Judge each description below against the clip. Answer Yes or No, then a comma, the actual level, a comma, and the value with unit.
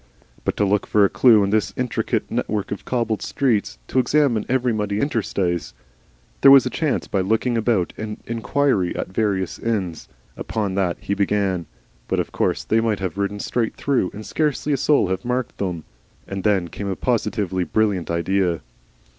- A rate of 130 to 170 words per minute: No, average, 180 wpm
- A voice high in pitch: No, low, 105 Hz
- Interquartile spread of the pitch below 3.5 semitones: No, average, 3.9 semitones